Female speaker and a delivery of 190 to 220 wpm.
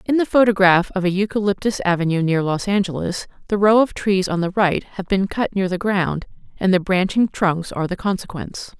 Yes: female; fast, 205 wpm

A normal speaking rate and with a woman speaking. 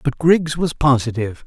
No: average, 165 wpm; male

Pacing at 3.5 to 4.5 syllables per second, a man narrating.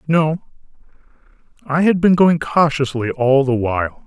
Yes: 4.4 syllables/s; male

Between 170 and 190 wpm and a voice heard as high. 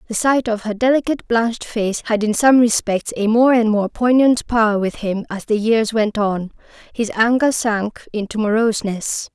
Yes: average, 185 wpm; high, 225 Hz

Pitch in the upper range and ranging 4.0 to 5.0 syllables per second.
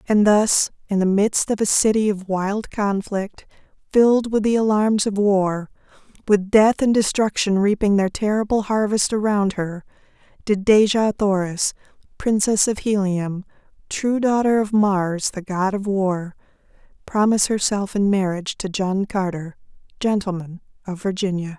Yes: high, 200 Hz; 4.4 syllables/s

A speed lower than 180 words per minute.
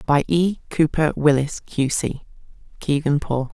Yes: slow, 135 wpm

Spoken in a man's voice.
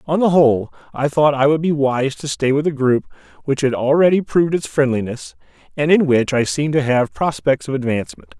Yes: male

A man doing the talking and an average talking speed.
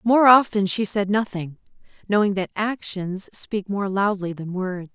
No: female; average, 160 wpm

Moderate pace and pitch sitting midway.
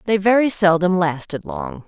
Yes: average, 160 wpm; medium, 165 Hz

